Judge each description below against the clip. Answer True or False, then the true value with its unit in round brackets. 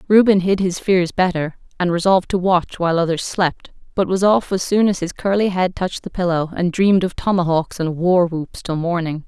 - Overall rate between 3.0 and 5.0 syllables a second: False (5.3 syllables/s)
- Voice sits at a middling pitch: True (180 Hz)